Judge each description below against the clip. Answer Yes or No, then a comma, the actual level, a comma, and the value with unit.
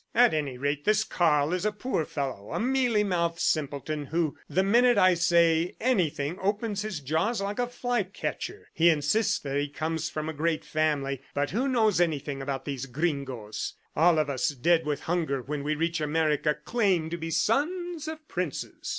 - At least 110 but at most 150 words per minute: No, average, 185 wpm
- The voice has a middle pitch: Yes, medium, 165 Hz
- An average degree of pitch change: No, wide, 6.0 semitones